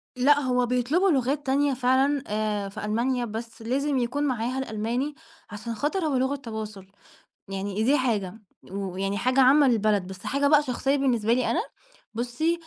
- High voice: Yes, very high, 250 Hz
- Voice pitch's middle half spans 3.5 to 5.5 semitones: Yes, average, 4.2 semitones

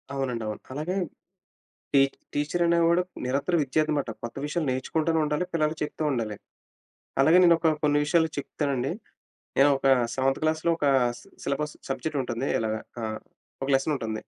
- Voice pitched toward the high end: No, medium, 145 Hz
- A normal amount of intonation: Yes, average, 3.4 semitones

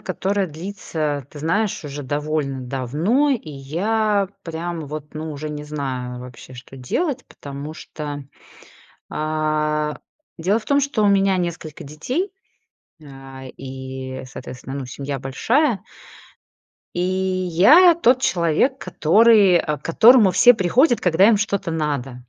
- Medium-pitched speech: Yes, medium, 160 Hz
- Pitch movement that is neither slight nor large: No, wide, 6.2 semitones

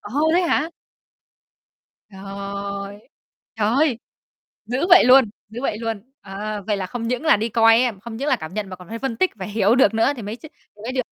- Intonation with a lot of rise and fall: No, average, 3.9 semitones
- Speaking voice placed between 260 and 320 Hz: No, high, 225 Hz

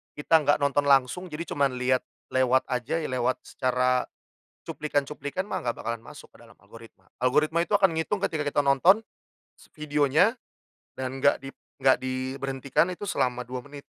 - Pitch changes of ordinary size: Yes, average, 3.1 semitones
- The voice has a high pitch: No, medium, 140 Hz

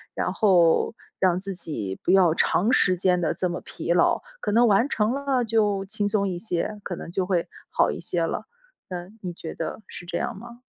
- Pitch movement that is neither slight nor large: Yes, average, 3.6 semitones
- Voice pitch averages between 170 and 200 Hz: Yes, high, 190 Hz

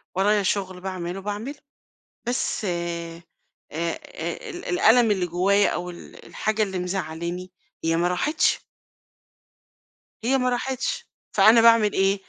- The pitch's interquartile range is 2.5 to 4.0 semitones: No, average, 4.5 semitones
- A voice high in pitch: Yes, high, 195 Hz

